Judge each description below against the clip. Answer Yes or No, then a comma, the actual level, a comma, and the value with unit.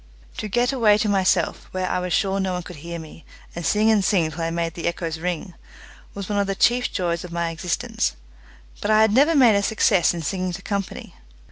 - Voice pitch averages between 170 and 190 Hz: Yes, medium, 185 Hz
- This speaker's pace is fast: Yes, fast, 230 wpm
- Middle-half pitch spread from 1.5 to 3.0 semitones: No, average, 3.4 semitones